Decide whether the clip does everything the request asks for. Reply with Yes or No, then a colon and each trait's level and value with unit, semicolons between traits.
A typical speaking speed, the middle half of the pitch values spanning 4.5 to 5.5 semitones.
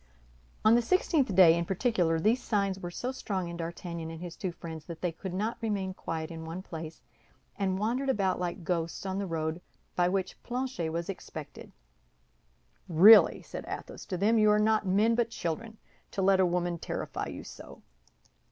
No: average, 185 wpm; average, 4.1 semitones